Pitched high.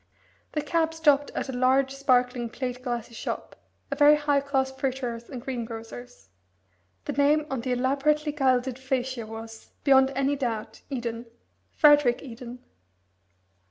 Yes: very high, 260 Hz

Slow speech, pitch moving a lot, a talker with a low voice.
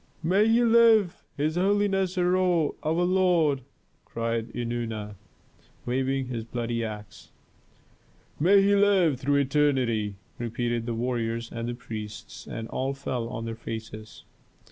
Yes: slow, 120 wpm; wide, 7.5 semitones; low, 130 Hz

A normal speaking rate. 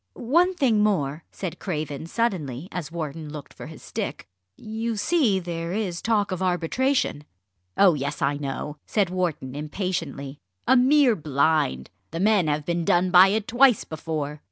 Yes: average, 155 wpm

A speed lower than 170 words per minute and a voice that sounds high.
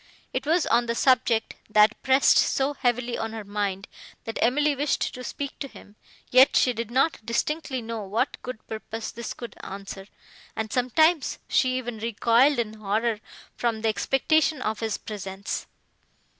Yes: average, 160 wpm; high, 235 Hz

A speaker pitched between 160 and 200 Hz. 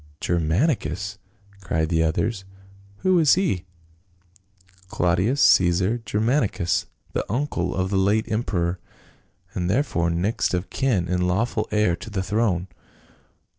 No: very low, 95 Hz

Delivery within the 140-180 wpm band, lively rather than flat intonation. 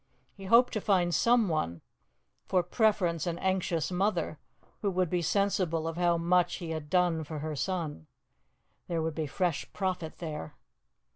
No: average, 155 wpm; average, 2.9 semitones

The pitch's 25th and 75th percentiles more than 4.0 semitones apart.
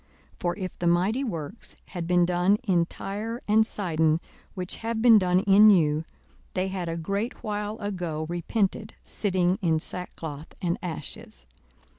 No: average, 3.4 semitones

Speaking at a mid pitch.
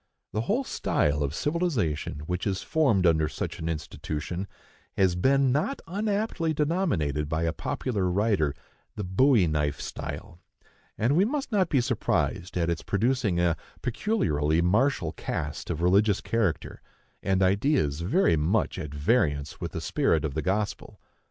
No: very low, 95 Hz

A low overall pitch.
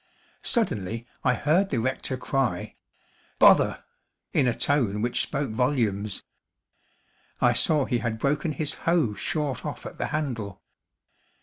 Yes: low, 130 Hz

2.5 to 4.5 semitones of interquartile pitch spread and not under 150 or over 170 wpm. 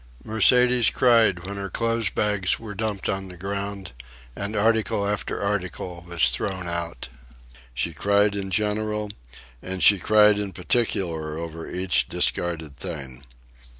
No: average, 3.3 semitones; slow, 135 wpm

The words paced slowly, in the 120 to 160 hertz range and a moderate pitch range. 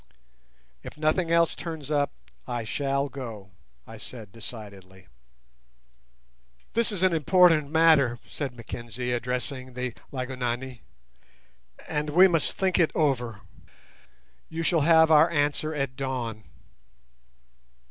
Yes: slow, 115 wpm; medium, 140 Hz; average, 4.9 semitones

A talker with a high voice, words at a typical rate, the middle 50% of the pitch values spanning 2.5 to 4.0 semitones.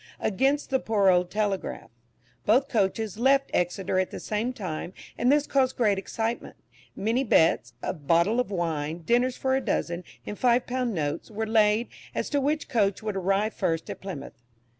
No: high, 215 Hz; average, 175 wpm; average, 5.2 semitones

